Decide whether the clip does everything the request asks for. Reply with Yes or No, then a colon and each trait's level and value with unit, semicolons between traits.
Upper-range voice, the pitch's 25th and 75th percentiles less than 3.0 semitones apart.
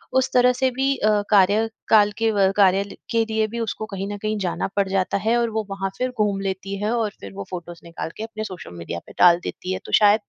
Yes: high, 205 Hz; narrow, 2.6 semitones